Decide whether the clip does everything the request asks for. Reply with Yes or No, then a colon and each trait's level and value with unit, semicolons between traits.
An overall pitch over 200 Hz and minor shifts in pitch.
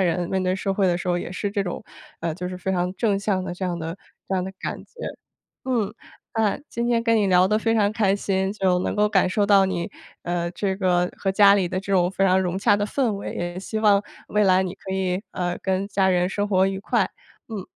No: high, 190 Hz; narrow, 1.9 semitones